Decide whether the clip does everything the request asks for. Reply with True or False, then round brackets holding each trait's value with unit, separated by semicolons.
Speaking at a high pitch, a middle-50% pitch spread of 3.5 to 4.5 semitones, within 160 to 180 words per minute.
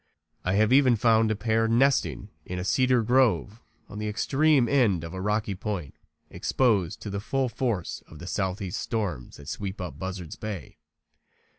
False (105 Hz; 4.2 semitones; 170 wpm)